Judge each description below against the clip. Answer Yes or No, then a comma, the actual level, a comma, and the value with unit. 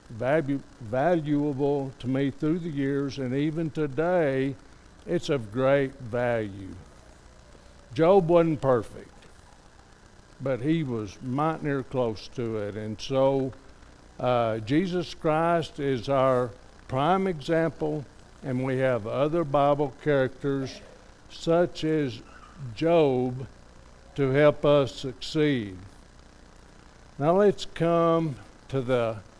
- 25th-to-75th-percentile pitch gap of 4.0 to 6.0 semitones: Yes, average, 4.7 semitones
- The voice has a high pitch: No, low, 135 Hz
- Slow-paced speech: Yes, slow, 105 wpm